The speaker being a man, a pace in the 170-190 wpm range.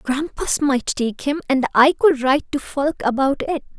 No: female; average, 175 wpm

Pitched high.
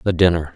No: very low, 85 Hz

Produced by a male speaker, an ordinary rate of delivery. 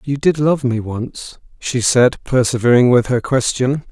Yes: male; average, 170 wpm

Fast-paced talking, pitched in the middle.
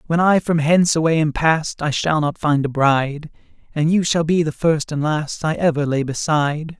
Yes: fast, 220 wpm; medium, 155 Hz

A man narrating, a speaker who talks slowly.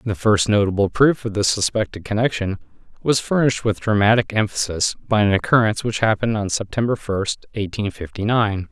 No: male; average, 165 wpm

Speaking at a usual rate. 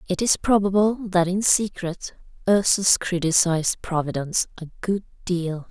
No: slow, 125 wpm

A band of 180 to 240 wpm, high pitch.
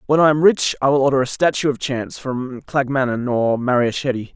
No: fast, 205 wpm; low, 135 Hz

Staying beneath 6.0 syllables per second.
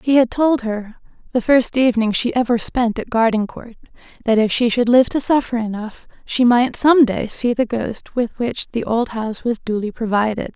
Yes: 4.9 syllables/s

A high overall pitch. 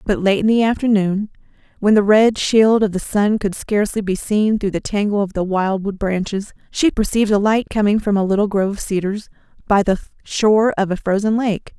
Yes: high, 205 Hz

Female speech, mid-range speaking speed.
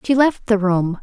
No: female; fast, 235 wpm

